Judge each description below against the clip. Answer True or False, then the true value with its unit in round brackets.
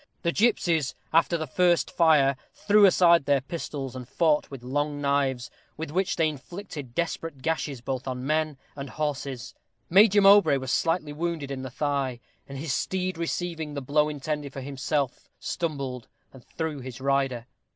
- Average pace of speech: True (160 wpm)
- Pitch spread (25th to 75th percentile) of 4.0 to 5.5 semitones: False (3.6 semitones)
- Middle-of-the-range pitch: True (145 Hz)